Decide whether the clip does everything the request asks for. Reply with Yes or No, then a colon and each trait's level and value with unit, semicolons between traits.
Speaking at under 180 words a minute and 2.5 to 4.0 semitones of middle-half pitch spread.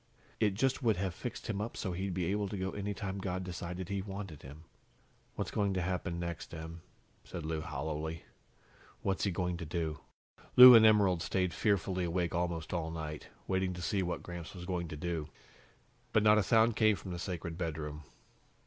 No: average, 195 wpm; average, 3.0 semitones